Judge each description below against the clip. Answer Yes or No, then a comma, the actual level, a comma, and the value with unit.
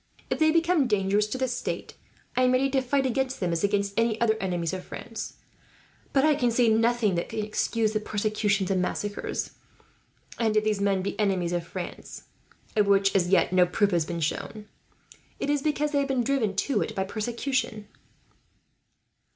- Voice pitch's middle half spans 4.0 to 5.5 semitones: Yes, average, 4.5 semitones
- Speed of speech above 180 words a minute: Yes, average, 190 wpm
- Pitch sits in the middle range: No, high, 215 Hz